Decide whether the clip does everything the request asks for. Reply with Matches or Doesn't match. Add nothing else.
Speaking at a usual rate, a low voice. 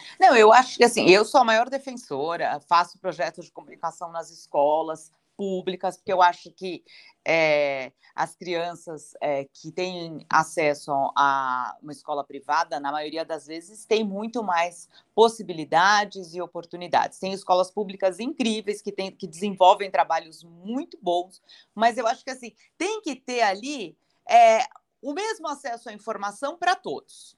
Doesn't match